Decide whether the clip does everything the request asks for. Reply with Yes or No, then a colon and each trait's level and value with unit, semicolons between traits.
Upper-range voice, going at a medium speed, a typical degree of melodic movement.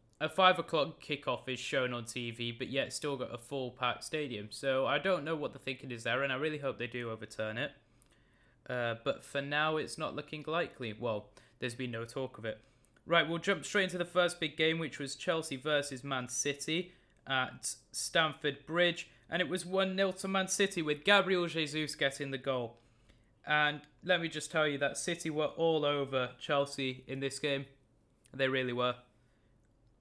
No: medium, 140 Hz; average, 195 wpm; average, 4.3 semitones